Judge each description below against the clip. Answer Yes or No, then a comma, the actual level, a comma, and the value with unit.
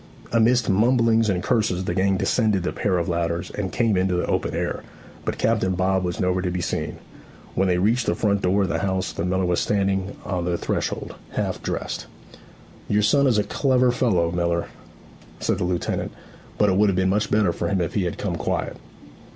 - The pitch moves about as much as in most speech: Yes, average, 3.0 semitones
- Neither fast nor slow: No, fast, 210 wpm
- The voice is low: Yes, very low, 95 Hz